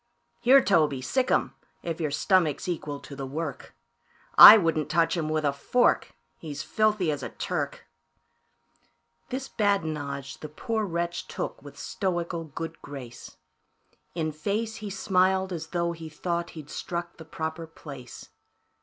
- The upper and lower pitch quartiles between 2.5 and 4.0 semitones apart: Yes, average, 3.7 semitones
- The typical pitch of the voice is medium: Yes, medium, 165 Hz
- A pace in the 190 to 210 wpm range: No, average, 145 wpm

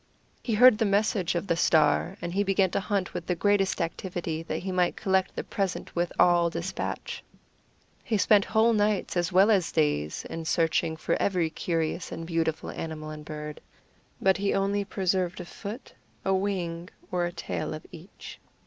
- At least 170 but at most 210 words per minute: Yes, average, 180 wpm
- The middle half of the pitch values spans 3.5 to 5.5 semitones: No, average, 3.1 semitones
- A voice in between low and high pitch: Yes, medium, 180 Hz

